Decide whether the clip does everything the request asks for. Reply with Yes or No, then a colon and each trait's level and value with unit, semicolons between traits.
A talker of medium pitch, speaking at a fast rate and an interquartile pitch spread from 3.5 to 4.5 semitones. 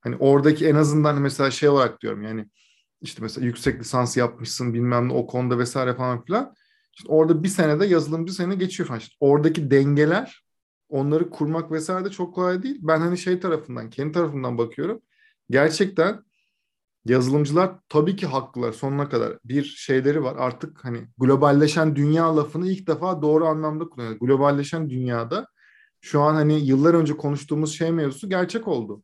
Yes: medium, 150 Hz; fast, 165 wpm; average, 4.1 semitones